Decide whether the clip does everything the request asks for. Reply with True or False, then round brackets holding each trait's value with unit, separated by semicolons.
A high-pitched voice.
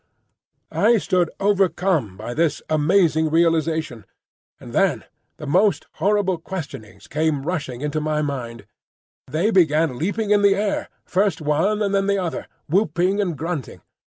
False (165 Hz)